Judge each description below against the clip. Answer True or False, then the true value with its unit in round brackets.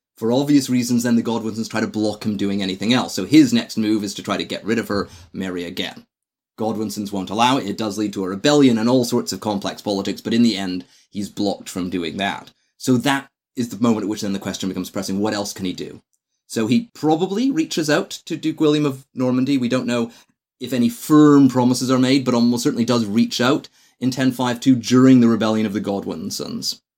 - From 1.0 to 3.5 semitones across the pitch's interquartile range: False (4.2 semitones)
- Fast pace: True (225 wpm)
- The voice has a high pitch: False (120 Hz)